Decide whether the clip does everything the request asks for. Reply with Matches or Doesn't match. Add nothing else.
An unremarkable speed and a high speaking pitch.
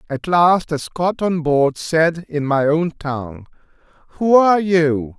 Doesn't match